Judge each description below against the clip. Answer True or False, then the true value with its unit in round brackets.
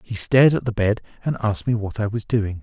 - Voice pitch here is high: False (110 Hz)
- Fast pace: True (275 wpm)